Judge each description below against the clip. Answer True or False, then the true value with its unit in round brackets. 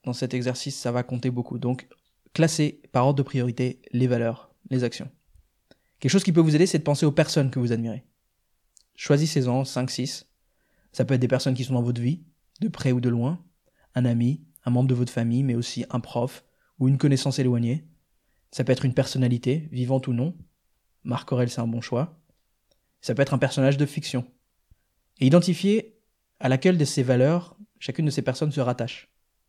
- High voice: False (130 Hz)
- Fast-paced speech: False (195 wpm)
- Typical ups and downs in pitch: True (3.5 semitones)